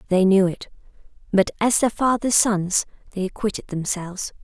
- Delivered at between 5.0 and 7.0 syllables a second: Yes, 5.1 syllables/s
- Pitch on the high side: Yes, high, 200 Hz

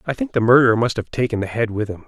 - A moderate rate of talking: No, fast, 320 wpm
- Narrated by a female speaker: No, male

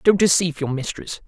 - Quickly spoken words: No, average, 190 wpm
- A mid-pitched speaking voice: Yes, medium, 160 Hz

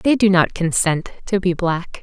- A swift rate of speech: Yes, fast, 210 wpm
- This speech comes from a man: No, female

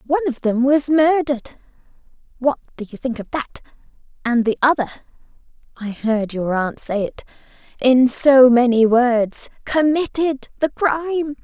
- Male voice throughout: No, female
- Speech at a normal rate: No, slow, 130 wpm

